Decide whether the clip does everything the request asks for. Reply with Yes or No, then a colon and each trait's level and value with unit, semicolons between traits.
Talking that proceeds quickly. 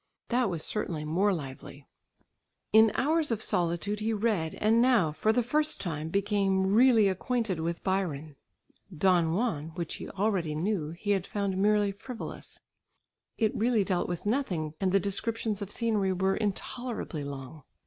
No: average, 155 wpm